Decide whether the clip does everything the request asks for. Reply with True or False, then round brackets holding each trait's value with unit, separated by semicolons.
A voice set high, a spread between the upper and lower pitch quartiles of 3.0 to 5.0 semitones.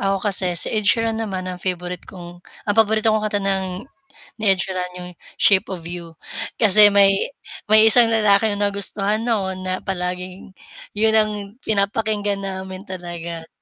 False (195 Hz; 2.6 semitones)